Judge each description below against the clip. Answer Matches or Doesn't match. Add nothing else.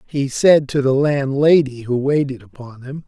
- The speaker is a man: Matches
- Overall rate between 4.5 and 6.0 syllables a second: Matches